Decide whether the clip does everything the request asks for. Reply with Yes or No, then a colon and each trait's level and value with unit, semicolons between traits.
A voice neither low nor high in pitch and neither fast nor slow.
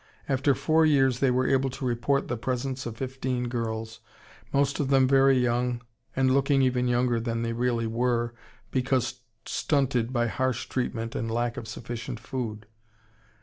No: low, 125 Hz; average, 160 wpm